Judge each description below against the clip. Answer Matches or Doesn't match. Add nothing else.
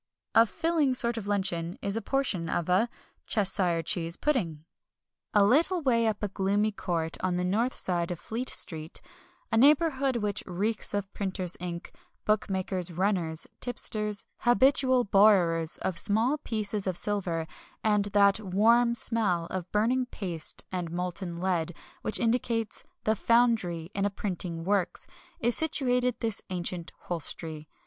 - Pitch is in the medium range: Doesn't match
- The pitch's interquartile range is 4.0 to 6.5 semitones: Matches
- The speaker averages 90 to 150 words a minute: Matches